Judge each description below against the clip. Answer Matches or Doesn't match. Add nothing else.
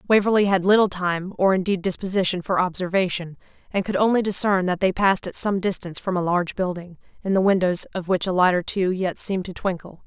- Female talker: Matches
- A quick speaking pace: Matches